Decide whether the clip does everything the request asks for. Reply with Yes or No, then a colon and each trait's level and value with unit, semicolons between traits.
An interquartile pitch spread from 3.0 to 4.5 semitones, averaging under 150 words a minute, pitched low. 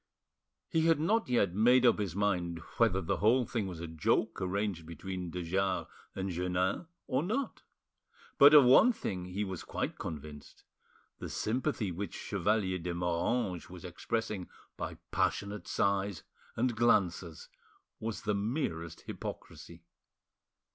No: average, 4.9 semitones; average, 140 wpm; low, 100 Hz